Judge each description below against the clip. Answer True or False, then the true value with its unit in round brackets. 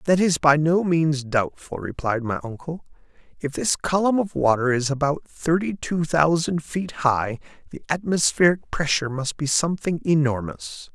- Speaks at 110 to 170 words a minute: True (155 wpm)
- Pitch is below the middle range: False (150 Hz)